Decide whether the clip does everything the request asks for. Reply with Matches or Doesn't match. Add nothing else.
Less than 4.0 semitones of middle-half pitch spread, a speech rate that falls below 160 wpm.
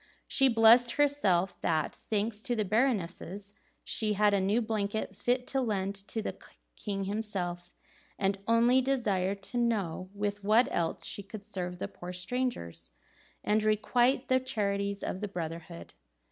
Matches